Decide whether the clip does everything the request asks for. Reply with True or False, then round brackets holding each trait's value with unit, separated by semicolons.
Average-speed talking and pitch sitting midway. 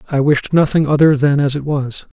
False (220 wpm; 145 Hz)